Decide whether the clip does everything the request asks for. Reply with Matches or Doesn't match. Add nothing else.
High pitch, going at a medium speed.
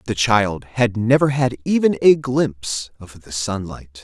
Doesn't match